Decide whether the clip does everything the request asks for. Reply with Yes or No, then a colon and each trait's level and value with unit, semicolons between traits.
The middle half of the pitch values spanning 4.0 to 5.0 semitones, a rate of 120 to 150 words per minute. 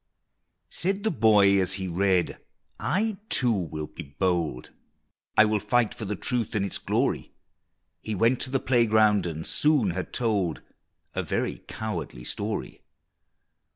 Yes: average, 4.5 semitones; average, 145 wpm